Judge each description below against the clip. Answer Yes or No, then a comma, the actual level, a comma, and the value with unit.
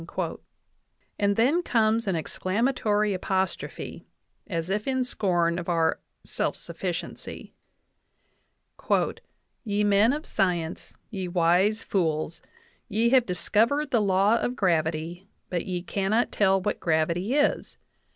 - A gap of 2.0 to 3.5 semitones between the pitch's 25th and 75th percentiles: No, average, 4.2 semitones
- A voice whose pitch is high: Yes, high, 195 Hz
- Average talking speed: No, slow, 115 wpm